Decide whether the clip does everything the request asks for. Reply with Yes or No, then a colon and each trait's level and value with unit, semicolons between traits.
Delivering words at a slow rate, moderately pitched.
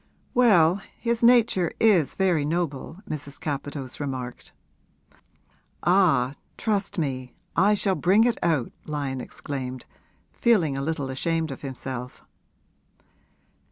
Yes: slow, 110 wpm; medium, 160 Hz